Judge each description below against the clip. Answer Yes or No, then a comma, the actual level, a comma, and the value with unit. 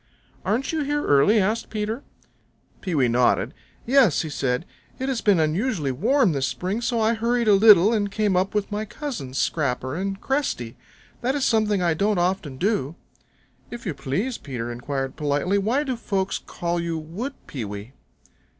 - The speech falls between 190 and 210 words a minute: No, average, 170 wpm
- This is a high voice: Yes, high, 195 Hz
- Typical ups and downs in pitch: No, wide, 7.9 semitones